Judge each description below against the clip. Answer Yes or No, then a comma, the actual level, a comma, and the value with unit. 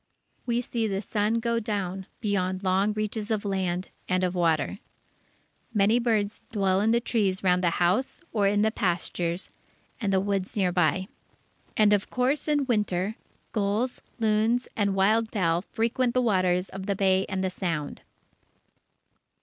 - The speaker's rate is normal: Yes, average, 160 wpm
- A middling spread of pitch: Yes, average, 3.0 semitones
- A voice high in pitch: Yes, high, 200 Hz